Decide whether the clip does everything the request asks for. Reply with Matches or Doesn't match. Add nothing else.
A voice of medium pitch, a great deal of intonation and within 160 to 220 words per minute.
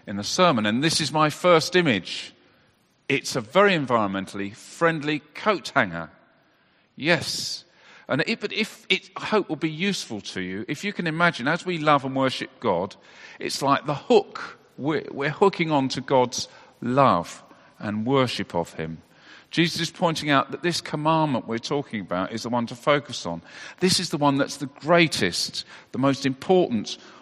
Matches